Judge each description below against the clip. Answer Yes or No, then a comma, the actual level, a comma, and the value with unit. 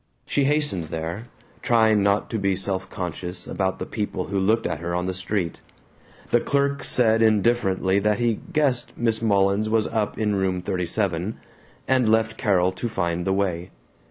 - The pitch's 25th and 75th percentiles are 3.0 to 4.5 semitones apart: Yes, average, 3.4 semitones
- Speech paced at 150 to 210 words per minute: Yes, average, 170 wpm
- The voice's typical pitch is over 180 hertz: No, low, 100 Hz